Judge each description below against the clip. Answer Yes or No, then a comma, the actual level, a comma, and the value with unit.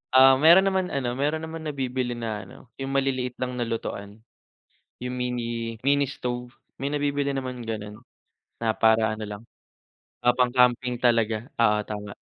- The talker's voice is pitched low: Yes, low, 125 Hz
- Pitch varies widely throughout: No, average, 2.9 semitones